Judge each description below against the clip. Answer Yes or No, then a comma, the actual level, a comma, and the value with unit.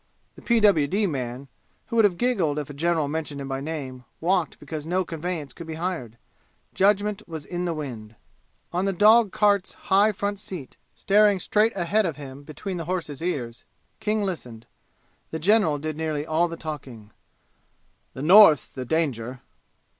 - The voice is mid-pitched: Yes, medium, 165 Hz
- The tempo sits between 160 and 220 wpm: Yes, average, 165 wpm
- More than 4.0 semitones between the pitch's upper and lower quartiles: Yes, wide, 5.5 semitones